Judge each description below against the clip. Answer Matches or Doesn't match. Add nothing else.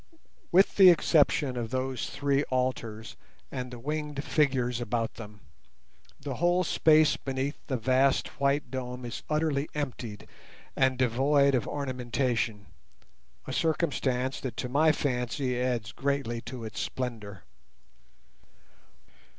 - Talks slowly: Matches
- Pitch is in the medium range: Doesn't match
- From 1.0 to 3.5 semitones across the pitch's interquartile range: Matches